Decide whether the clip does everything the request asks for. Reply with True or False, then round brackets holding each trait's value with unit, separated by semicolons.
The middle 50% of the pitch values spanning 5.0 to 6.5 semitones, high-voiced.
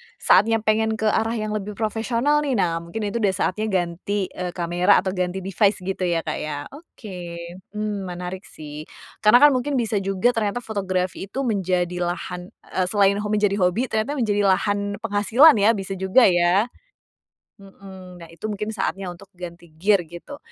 False (3.3 semitones; 195 Hz)